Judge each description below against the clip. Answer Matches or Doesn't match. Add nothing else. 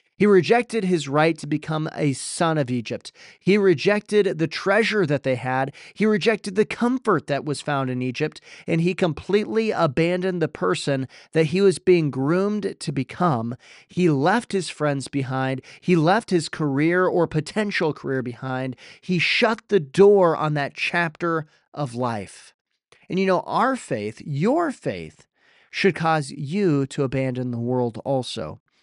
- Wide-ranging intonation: Matches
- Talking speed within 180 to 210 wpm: Doesn't match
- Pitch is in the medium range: Matches